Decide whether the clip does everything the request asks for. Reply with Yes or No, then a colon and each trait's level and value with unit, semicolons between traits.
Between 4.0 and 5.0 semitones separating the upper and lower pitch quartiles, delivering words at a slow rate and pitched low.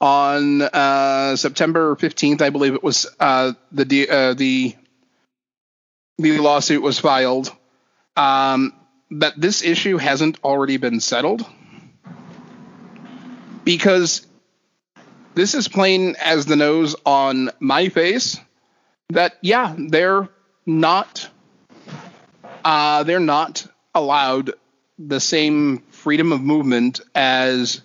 No: average, 4.3 semitones; slow, 105 wpm; medium, 150 Hz